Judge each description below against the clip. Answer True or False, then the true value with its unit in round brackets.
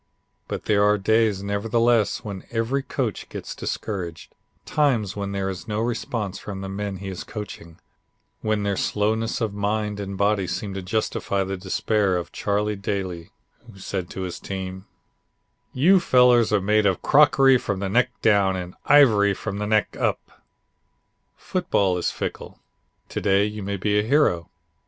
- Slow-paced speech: False (165 wpm)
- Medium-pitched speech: False (100 Hz)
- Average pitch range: False (2.3 semitones)